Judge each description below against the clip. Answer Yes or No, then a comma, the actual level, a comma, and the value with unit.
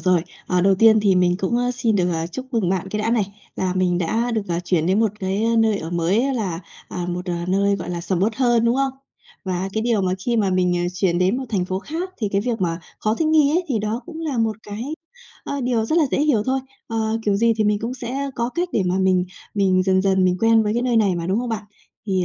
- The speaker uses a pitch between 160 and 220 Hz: Yes, high, 210 Hz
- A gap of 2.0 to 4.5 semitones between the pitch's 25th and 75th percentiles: Yes, average, 4.1 semitones